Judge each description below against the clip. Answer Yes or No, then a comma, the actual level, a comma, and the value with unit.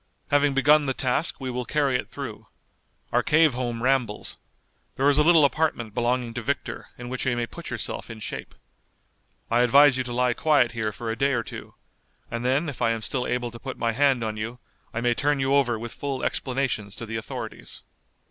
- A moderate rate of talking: No, fast, 215 wpm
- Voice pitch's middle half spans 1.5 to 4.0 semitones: Yes, average, 3.0 semitones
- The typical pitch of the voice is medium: No, low, 125 Hz